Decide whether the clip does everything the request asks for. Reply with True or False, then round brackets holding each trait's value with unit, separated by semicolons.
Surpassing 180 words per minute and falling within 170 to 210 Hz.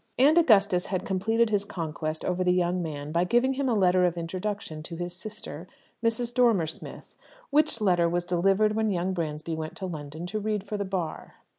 True (195 wpm; 185 Hz)